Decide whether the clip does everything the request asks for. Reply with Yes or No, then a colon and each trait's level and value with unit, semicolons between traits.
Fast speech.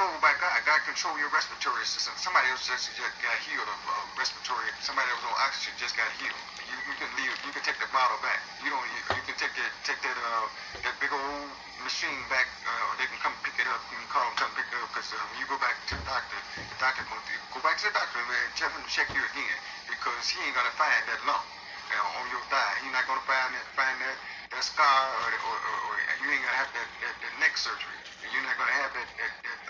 Yes: fast, 270 wpm